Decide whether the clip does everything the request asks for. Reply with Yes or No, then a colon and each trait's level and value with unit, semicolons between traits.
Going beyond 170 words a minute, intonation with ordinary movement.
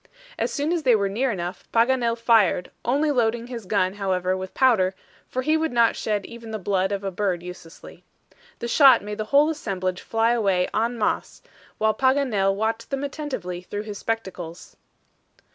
Yes: average, 180 wpm; average, 4.3 semitones